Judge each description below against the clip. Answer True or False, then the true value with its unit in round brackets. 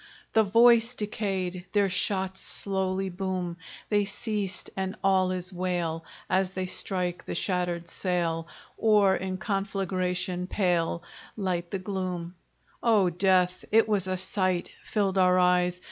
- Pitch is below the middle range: False (185 Hz)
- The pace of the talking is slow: True (130 wpm)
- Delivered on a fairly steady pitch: True (1.6 semitones)